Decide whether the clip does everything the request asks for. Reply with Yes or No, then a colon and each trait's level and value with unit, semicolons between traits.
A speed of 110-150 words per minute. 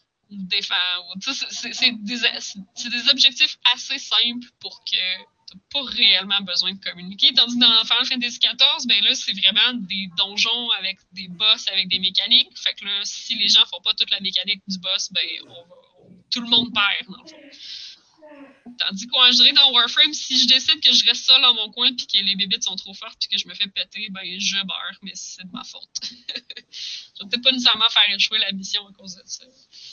No: fast, 220 wpm